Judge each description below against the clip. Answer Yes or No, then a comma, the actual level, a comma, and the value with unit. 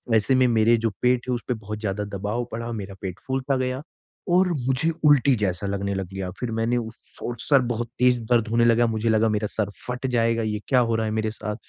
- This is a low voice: Yes, low, 115 Hz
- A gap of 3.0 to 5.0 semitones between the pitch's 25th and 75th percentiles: No, narrow, 2.6 semitones